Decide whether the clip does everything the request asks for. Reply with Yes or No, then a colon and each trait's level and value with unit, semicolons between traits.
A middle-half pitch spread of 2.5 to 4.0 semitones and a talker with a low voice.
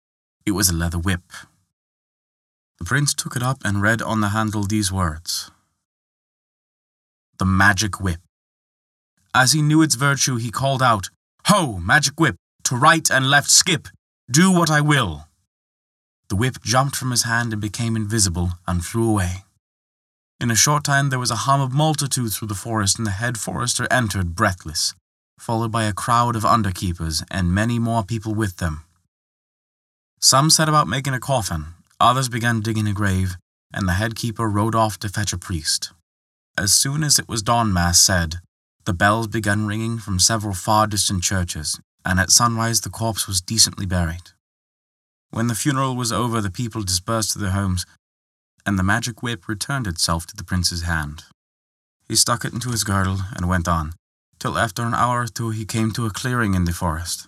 No: average, 4.7 semitones; low, 105 Hz